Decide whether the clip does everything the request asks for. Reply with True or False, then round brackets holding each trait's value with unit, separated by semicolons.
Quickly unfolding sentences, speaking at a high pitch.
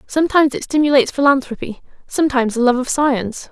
False (155 wpm; 265 Hz)